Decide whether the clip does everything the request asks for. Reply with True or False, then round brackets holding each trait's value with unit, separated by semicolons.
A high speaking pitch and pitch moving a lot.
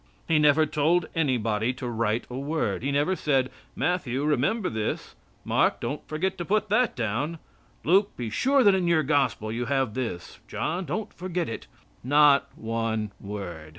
False (140 Hz; 6.7 semitones)